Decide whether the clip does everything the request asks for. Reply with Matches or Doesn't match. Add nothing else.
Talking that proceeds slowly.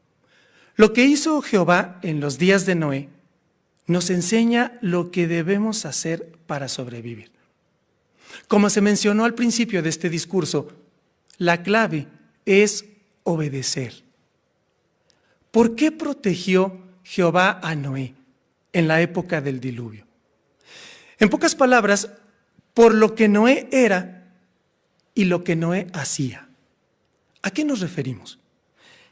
Matches